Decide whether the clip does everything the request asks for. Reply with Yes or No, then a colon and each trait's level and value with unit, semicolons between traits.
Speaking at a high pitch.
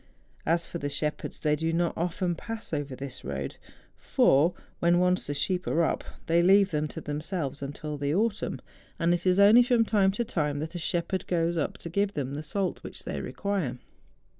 No: medium, 170 Hz